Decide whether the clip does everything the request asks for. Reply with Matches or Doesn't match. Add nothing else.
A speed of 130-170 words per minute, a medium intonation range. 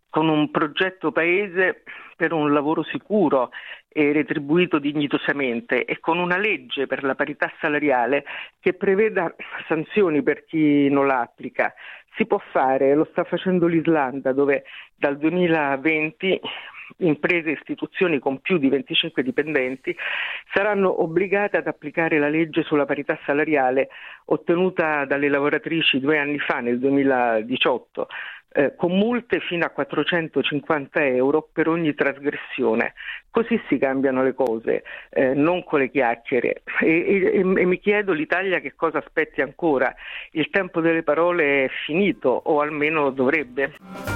Matches